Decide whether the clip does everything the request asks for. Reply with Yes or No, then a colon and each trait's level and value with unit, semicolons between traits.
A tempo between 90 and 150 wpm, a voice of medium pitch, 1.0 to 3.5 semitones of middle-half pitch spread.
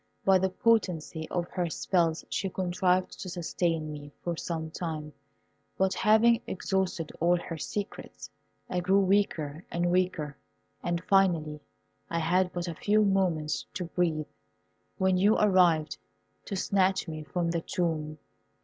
Yes: average, 140 wpm; medium, 175 Hz; average, 2.8 semitones